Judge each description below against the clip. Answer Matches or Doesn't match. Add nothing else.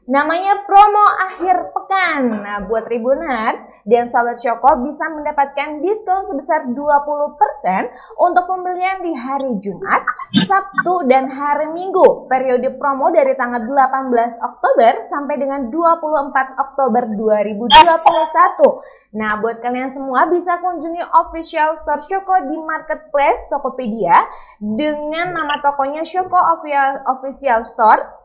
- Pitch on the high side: Matches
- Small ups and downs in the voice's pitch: Doesn't match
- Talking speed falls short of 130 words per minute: Matches